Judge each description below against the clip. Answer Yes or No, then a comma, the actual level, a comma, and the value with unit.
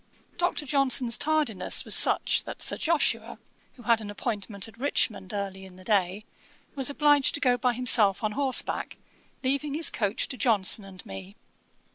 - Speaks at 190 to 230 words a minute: No, average, 165 wpm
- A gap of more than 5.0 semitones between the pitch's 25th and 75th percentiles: Yes, wide, 5.6 semitones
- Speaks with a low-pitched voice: No, high, 230 Hz